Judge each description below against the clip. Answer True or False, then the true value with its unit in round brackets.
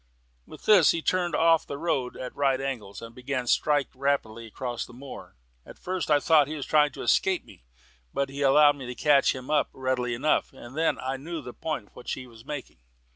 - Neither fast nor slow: False (225 wpm)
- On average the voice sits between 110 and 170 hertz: True (140 Hz)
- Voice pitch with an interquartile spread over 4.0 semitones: False (3.3 semitones)